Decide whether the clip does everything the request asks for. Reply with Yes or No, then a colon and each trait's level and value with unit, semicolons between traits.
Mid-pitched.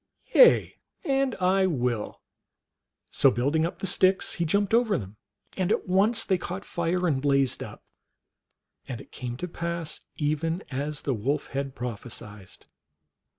Yes: medium, 160 Hz